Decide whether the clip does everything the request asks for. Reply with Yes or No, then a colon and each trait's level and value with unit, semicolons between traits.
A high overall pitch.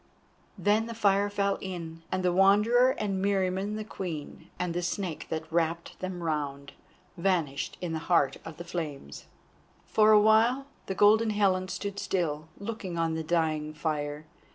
No: medium, 180 Hz